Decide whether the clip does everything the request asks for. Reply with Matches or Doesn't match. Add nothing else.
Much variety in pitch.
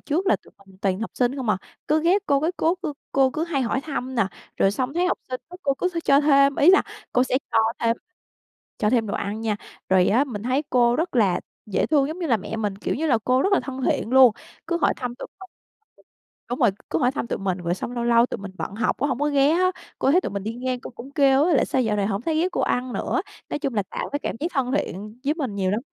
Doesn't match